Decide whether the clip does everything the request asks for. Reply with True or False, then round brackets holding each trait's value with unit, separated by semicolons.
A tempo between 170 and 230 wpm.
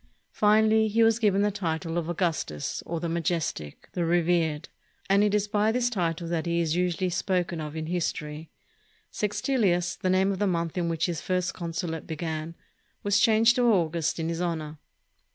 True (180 wpm)